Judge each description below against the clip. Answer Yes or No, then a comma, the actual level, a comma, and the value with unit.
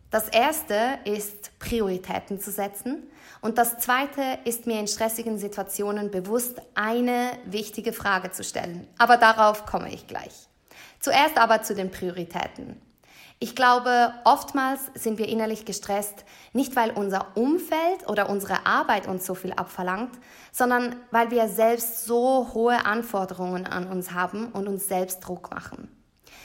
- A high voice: Yes, high, 220 Hz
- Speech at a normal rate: Yes, average, 145 wpm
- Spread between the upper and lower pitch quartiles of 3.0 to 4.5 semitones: Yes, average, 3.4 semitones